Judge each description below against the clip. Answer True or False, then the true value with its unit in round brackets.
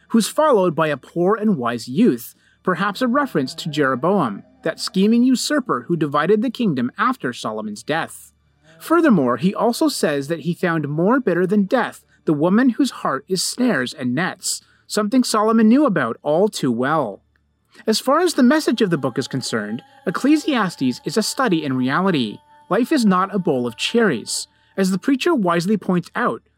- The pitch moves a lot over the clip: True (7.4 semitones)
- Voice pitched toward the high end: True (200 Hz)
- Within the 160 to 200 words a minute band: True (175 wpm)